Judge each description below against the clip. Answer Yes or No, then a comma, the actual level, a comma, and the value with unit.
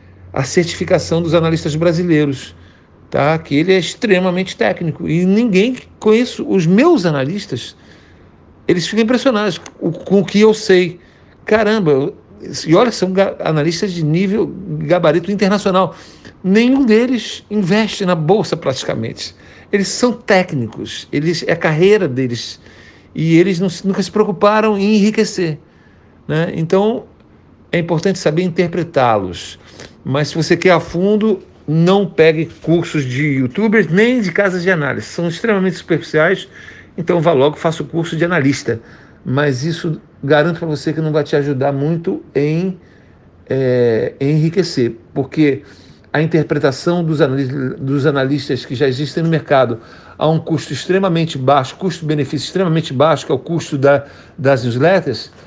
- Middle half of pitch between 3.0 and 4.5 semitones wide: No, average, 5.1 semitones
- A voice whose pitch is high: No, medium, 165 Hz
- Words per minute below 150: Yes, average, 140 wpm